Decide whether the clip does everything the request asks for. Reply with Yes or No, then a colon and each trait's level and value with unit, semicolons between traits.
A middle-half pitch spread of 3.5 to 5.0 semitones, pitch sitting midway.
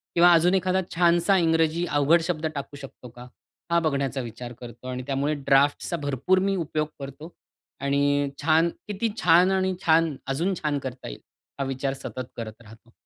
Yes: average, 4.0 semitones; medium, 150 Hz